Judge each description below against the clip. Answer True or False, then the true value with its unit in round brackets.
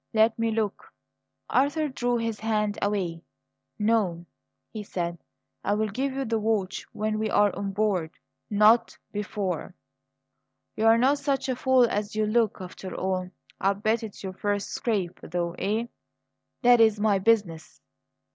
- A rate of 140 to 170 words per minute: True (150 wpm)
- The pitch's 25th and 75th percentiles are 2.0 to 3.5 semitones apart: True (2.6 semitones)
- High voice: True (215 Hz)